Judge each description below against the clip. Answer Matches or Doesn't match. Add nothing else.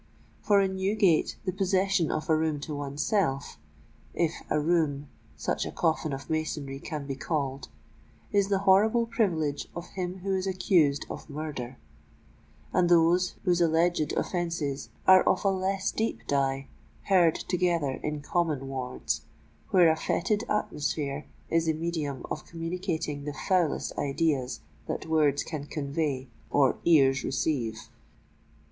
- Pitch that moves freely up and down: Doesn't match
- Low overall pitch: Doesn't match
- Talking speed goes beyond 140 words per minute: Doesn't match